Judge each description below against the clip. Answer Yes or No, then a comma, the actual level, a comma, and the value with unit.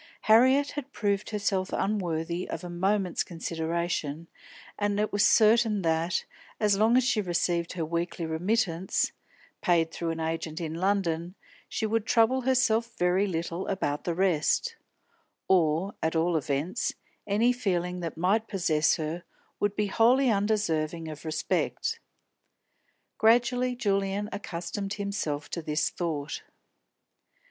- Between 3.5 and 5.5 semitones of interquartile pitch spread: Yes, average, 4.5 semitones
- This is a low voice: No, medium, 185 Hz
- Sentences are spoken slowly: Yes, slow, 130 wpm